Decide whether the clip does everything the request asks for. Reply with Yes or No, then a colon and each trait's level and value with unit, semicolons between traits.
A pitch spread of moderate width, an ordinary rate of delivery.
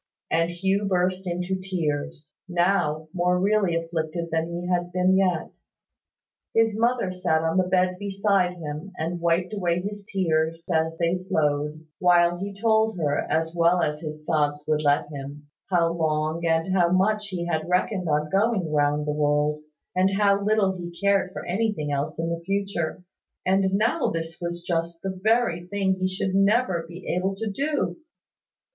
Yes: average, 3.0 semitones; average, 170 wpm